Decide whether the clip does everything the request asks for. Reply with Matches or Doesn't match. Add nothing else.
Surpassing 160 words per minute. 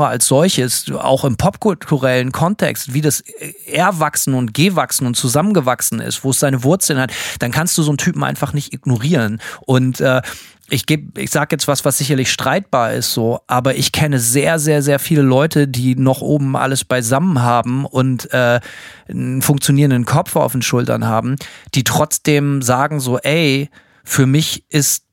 Matches